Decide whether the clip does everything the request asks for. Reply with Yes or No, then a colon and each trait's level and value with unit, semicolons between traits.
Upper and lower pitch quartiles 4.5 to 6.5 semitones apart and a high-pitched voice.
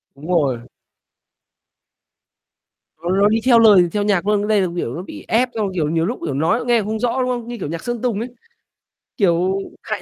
Yes: average, 5.0 semitones; high, 205 Hz